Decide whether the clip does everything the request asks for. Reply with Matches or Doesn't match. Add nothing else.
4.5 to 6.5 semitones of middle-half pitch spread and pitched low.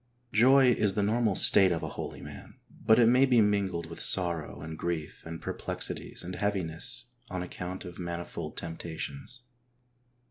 Matches